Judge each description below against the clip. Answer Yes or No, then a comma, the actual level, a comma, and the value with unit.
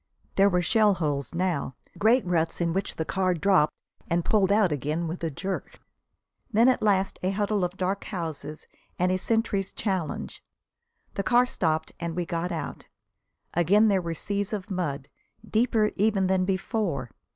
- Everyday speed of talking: Yes, average, 160 wpm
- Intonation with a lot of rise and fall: No, average, 3.3 semitones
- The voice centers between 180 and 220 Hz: Yes, medium, 185 Hz